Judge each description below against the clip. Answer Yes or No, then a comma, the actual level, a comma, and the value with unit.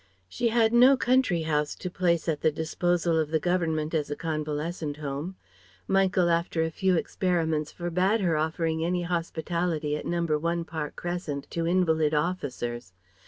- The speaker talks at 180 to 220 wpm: No, average, 160 wpm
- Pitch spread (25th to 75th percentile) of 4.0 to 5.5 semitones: No, narrow, 2.5 semitones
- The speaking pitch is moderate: Yes, medium, 165 Hz